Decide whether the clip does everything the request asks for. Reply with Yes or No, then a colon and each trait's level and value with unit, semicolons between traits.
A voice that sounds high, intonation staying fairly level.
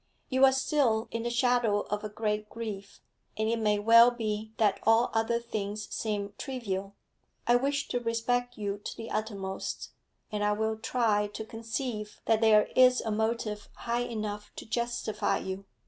Yes: high, 220 Hz; narrow, 2.2 semitones